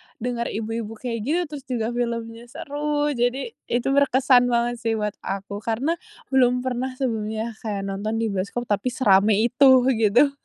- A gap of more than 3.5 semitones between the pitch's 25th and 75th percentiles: No, average, 2.9 semitones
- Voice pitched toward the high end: Yes, high, 235 Hz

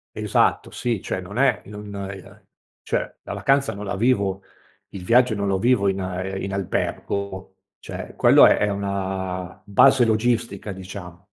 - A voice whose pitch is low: Yes, low, 100 Hz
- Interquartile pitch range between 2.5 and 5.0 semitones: Yes, average, 2.8 semitones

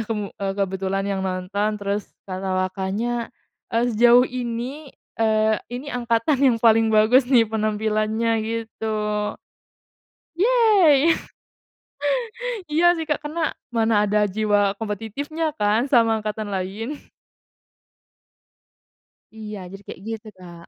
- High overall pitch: Yes, high, 220 Hz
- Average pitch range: Yes, average, 3.0 semitones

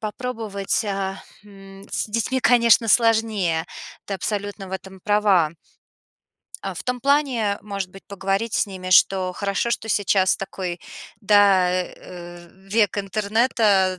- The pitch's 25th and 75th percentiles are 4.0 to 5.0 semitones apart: No, narrow, 2.6 semitones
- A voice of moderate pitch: No, high, 200 Hz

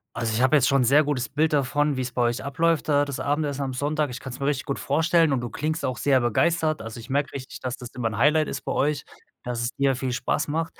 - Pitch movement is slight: No, average, 3.0 semitones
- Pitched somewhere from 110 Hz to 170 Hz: Yes, medium, 140 Hz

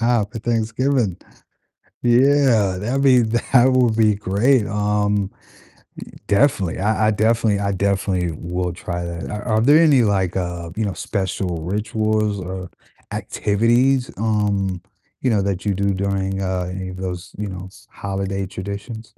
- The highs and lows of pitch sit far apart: No, average, 3.2 semitones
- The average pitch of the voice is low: Yes, low, 100 Hz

